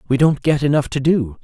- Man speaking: Yes, male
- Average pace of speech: No, fast, 250 wpm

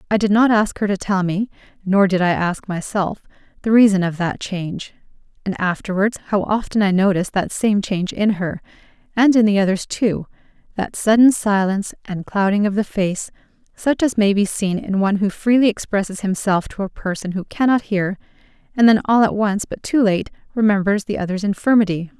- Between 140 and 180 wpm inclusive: No, average, 190 wpm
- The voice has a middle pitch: No, high, 200 Hz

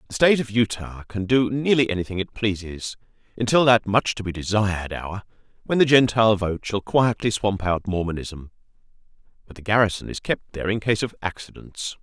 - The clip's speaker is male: Yes, male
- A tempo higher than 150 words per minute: Yes, average, 180 wpm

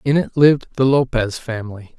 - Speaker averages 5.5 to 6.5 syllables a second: Yes, 5.6 syllables/s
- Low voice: Yes, low, 125 Hz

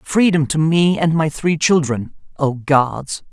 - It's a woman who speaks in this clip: No, male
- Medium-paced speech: Yes, average, 145 wpm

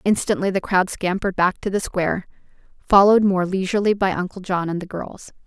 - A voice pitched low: No, high, 190 Hz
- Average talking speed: Yes, average, 185 wpm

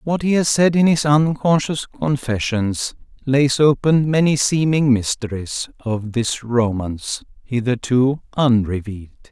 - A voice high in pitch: No, low, 130 Hz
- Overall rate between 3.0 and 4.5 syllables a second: Yes, 4.1 syllables/s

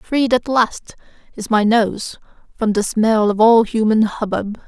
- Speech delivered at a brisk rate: No, average, 165 wpm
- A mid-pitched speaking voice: No, high, 220 Hz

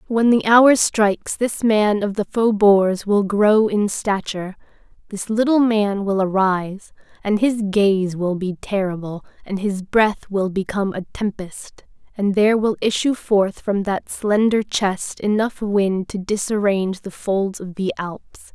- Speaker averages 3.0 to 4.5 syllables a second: Yes, 4.1 syllables/s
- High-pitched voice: Yes, high, 205 Hz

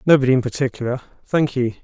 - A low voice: Yes, low, 130 Hz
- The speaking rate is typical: Yes, average, 165 wpm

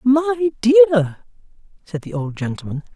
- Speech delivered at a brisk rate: No, slow, 120 wpm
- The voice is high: Yes, high, 205 Hz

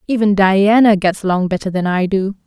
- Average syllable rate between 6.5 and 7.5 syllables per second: No, 5.3 syllables/s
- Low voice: No, high, 195 Hz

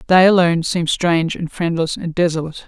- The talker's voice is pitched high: No, medium, 170 Hz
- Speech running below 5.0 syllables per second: No, 6.5 syllables/s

